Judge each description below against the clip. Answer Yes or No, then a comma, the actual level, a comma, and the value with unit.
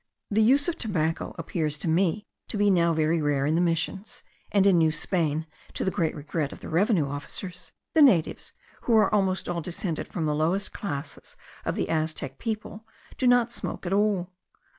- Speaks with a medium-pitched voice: Yes, medium, 175 Hz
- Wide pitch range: No, average, 4.6 semitones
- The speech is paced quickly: No, average, 190 wpm